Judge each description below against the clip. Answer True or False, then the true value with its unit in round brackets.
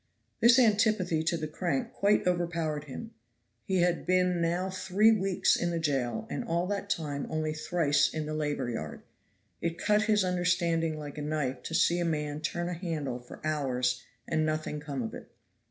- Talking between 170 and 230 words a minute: True (185 wpm)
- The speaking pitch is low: False (165 Hz)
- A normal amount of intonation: True (3.4 semitones)